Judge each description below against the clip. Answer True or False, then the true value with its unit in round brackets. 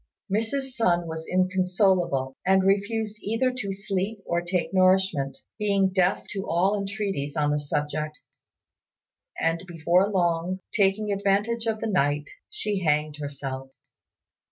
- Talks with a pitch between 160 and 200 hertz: True (185 Hz)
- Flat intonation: False (4.1 semitones)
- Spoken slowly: True (130 wpm)